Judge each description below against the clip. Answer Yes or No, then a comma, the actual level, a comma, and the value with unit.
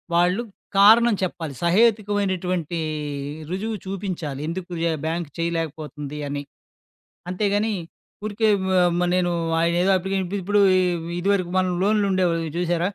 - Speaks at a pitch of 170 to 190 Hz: Yes, medium, 185 Hz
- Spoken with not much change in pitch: No, average, 3.2 semitones